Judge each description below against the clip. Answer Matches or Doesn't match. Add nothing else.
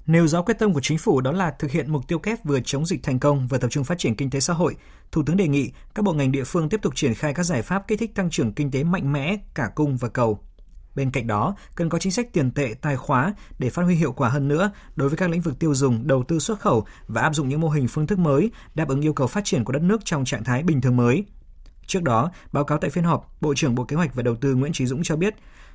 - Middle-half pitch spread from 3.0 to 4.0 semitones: Doesn't match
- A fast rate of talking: Matches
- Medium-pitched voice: Matches